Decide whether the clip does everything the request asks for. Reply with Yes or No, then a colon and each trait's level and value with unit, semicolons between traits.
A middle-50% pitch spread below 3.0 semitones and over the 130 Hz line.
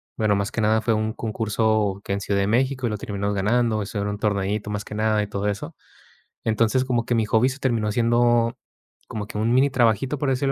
No: narrow, 2.5 semitones; low, 110 Hz